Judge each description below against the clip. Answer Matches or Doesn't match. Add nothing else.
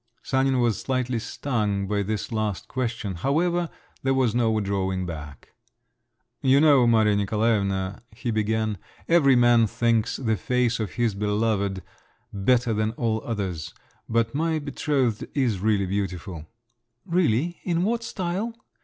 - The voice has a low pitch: Matches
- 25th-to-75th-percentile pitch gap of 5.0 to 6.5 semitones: Doesn't match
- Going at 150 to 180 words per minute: Doesn't match